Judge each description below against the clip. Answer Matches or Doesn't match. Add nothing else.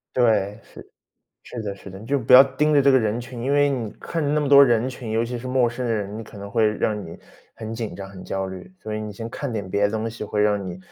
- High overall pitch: Doesn't match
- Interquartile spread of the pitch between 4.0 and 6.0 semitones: Doesn't match